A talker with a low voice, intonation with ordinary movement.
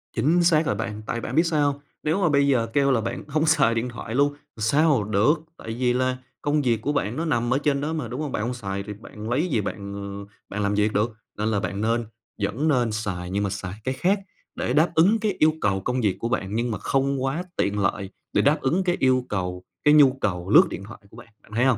No: low, 120 Hz; wide, 5.8 semitones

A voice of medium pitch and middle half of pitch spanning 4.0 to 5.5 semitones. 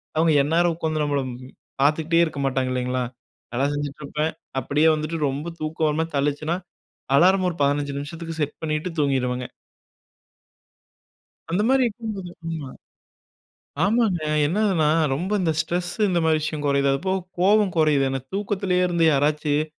No: medium, 155 Hz; average, 3.4 semitones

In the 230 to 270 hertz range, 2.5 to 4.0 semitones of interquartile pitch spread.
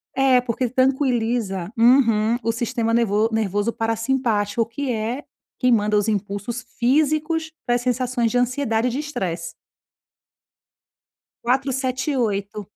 Yes: high, 235 Hz; average, 3.0 semitones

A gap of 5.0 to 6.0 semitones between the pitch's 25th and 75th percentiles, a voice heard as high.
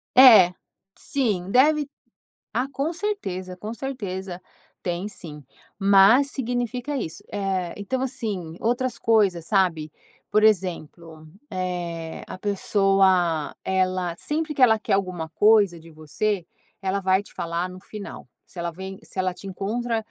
No: average, 4.3 semitones; high, 195 Hz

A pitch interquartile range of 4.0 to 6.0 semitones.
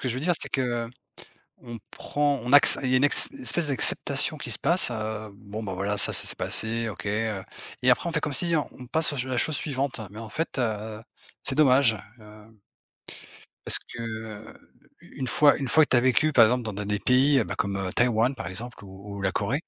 Yes: average, 4.3 semitones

